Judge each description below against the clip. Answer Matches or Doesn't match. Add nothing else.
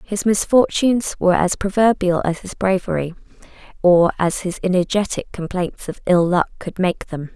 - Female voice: Matches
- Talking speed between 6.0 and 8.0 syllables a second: Doesn't match